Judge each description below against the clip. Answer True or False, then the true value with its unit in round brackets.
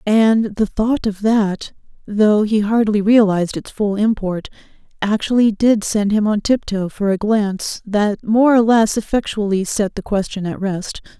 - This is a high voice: True (210 Hz)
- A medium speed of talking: True (160 wpm)